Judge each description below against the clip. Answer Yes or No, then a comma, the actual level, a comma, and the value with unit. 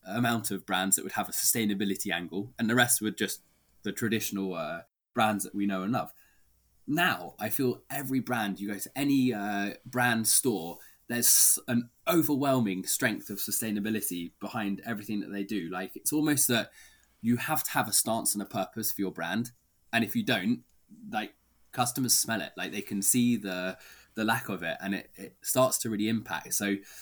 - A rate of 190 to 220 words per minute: Yes, average, 195 wpm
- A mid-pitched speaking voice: No, low, 110 Hz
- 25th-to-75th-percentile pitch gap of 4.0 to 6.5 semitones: No, average, 3.6 semitones